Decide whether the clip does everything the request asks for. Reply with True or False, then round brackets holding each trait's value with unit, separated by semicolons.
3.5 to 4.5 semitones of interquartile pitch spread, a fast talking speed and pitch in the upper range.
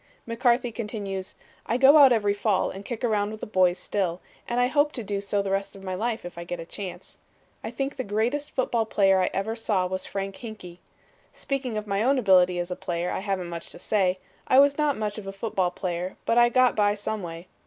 True (4.1 semitones; 235 wpm; 205 Hz)